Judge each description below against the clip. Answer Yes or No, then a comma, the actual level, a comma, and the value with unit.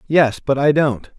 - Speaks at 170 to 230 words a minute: Yes, fast, 205 wpm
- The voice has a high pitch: No, medium, 140 Hz